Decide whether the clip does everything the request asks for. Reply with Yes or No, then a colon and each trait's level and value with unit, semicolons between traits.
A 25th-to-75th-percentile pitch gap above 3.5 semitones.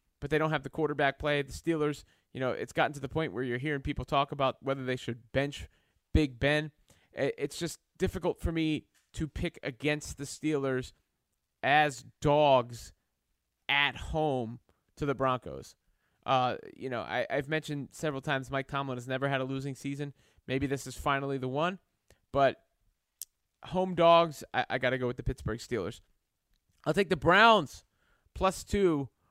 No: average, 2.9 semitones